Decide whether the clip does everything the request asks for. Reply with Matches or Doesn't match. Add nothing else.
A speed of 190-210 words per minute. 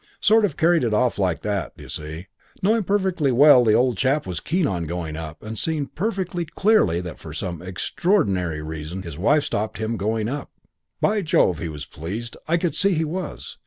Matches